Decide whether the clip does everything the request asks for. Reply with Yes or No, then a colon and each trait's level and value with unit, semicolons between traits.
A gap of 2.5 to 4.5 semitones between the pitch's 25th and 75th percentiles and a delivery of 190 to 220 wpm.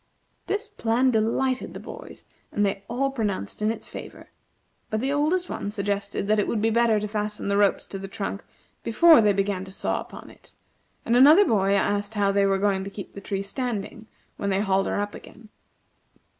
Yes: average, 2.9 semitones; average, 200 wpm